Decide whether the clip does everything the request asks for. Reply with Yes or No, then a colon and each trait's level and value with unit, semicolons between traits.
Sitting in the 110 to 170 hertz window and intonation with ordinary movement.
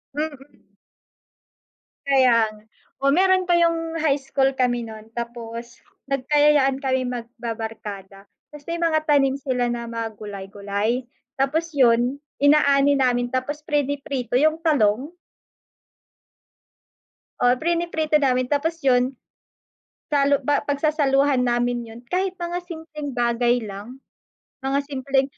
No: very high, 270 Hz; average, 3.7 semitones